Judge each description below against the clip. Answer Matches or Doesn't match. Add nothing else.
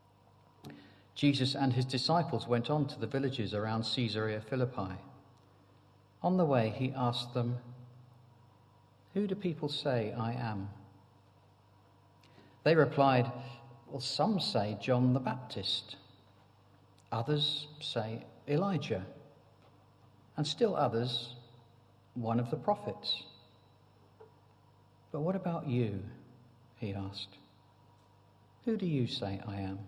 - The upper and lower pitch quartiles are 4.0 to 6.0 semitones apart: Matches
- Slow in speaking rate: Matches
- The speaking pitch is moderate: Doesn't match